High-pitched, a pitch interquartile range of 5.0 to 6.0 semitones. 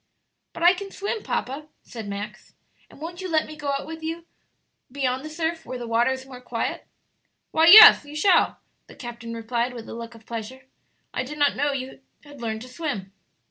Yes: very high, 265 Hz; wide, 5.4 semitones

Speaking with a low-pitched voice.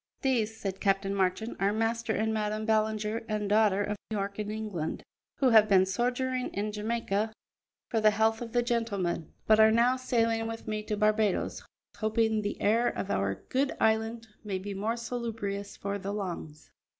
No: high, 215 Hz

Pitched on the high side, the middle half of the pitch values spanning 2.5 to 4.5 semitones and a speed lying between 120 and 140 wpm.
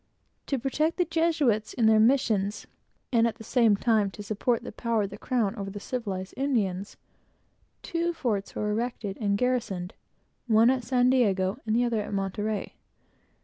No: high, 225 Hz; average, 3.6 semitones; average, 170 wpm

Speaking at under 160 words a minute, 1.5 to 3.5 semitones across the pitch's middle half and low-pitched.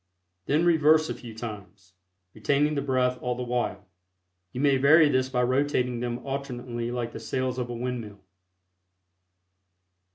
Yes: average, 150 wpm; average, 2.7 semitones; low, 125 Hz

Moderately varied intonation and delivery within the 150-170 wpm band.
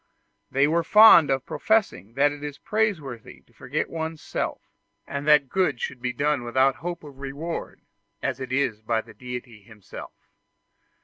Yes: average, 4.3 semitones; average, 165 wpm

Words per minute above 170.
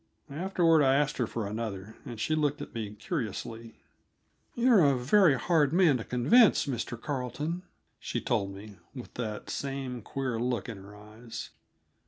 No: average, 160 wpm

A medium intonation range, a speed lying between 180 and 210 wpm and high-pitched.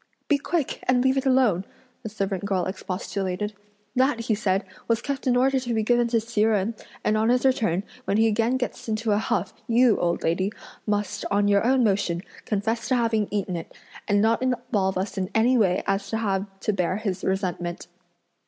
Yes: average, 3.7 semitones; average, 200 wpm; high, 215 Hz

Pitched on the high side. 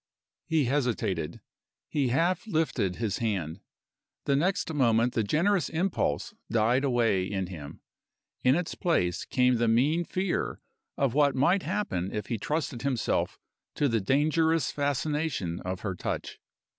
No: low, 130 Hz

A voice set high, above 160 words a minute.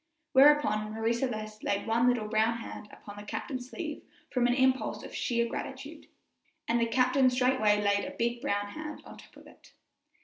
Yes: high, 235 Hz; average, 175 wpm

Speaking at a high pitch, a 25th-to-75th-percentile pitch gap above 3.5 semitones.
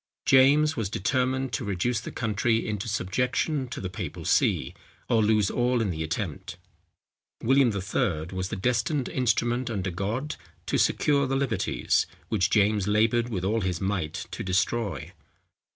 No: low, 110 Hz; average, 4.7 semitones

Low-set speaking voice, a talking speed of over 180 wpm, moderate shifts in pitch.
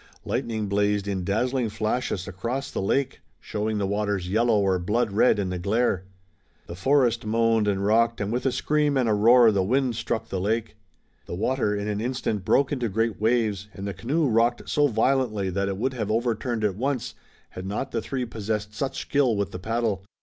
Yes: low, 110 Hz; average, 200 wpm; average, 3.2 semitones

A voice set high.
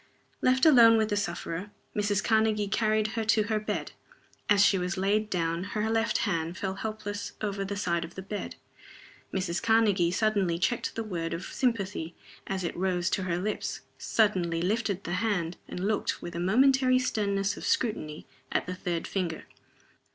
Yes: high, 200 Hz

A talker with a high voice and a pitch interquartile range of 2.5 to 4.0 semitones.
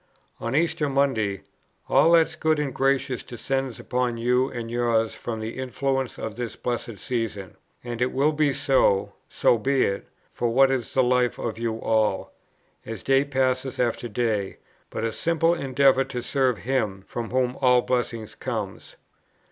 No: low, 125 Hz; average, 2.9 semitones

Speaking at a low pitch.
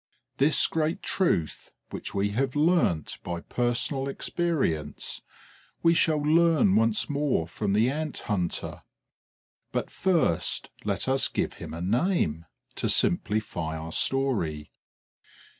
Yes: low, 120 Hz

